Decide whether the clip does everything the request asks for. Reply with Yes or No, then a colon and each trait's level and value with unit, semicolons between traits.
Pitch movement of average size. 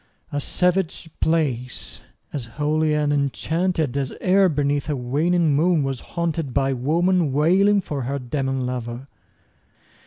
Yes: average, 3.9 semitones